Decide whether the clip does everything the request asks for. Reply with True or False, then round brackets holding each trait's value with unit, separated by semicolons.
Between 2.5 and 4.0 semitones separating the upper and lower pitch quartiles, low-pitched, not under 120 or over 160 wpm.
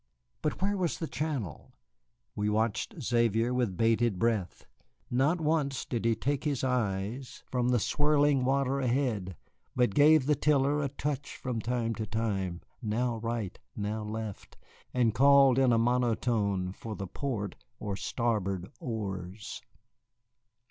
False (4.4 semitones; 120 Hz; 140 wpm)